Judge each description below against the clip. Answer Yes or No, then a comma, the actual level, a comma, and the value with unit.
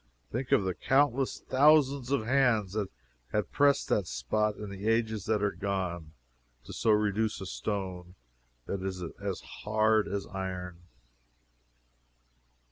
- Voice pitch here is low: Yes, low, 105 Hz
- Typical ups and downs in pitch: Yes, average, 3.3 semitones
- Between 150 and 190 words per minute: No, slow, 135 wpm